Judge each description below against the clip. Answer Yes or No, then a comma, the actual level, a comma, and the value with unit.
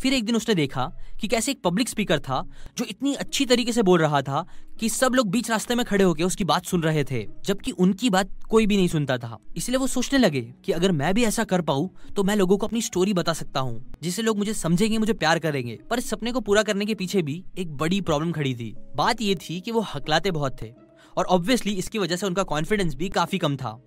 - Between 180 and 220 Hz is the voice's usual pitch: Yes, medium, 185 Hz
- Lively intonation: Yes, wide, 6.2 semitones